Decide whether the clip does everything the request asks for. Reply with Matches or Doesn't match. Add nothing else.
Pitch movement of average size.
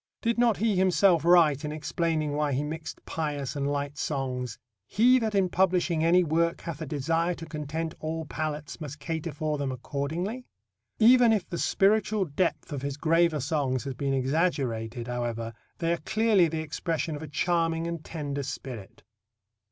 Matches